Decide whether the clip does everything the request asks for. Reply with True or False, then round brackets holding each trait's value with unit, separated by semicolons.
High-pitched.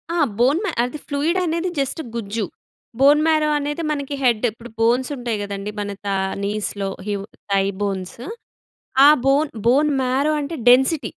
True (260 Hz)